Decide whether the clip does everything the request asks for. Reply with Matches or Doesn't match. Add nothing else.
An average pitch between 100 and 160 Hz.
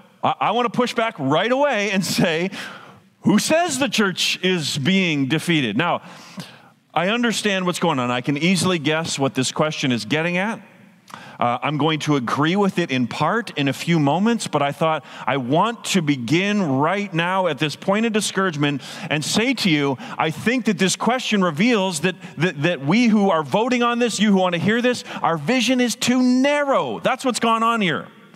Doesn't match